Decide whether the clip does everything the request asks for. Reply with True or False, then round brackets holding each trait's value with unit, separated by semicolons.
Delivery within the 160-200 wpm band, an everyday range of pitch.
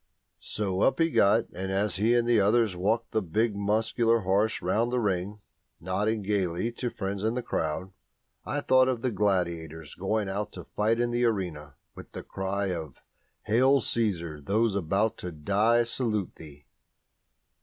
True (165 wpm; 3.8 semitones)